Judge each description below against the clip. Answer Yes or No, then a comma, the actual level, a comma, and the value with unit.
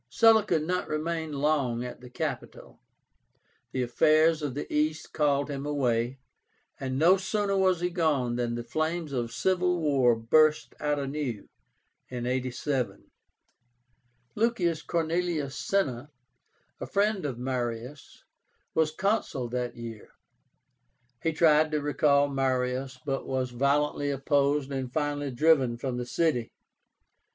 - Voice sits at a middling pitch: Yes, medium, 145 Hz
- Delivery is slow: Yes, slow, 125 wpm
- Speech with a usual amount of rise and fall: Yes, average, 4.1 semitones